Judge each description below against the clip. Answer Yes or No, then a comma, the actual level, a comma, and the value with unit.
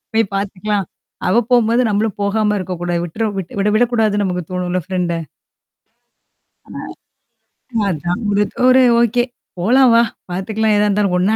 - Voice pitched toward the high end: Yes, high, 205 Hz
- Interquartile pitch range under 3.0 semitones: No, average, 3.3 semitones